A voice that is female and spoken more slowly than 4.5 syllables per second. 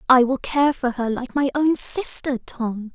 Yes: female; 4.0 syllables/s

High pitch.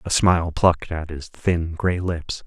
No: very low, 85 Hz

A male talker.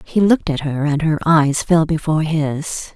No: female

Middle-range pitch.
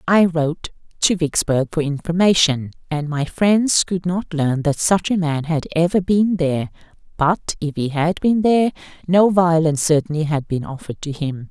Yes: medium, 165 Hz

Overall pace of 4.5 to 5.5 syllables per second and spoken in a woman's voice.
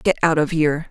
No: 7.0 syllables/s; female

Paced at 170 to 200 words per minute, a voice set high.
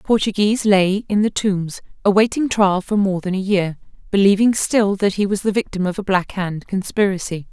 Yes: average, 190 wpm; high, 195 Hz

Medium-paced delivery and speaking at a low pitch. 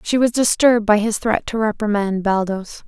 No: average, 190 wpm; high, 215 Hz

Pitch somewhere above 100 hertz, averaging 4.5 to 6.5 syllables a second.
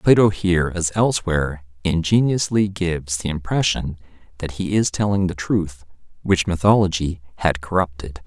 No: very low, 90 Hz; 5.0 syllables/s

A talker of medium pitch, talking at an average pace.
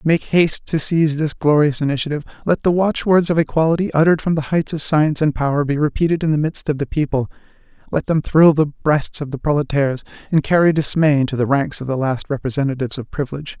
No: medium, 150 Hz; fast, 210 wpm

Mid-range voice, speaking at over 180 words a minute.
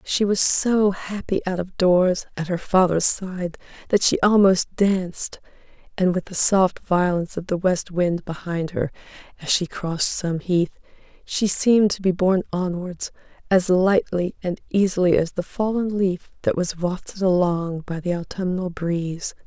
No: medium, 180 Hz; average, 165 wpm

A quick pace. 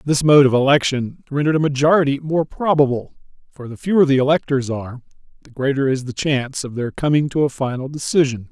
No: average, 190 wpm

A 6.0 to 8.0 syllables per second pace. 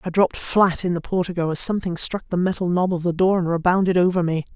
Yes: 6.5 syllables/s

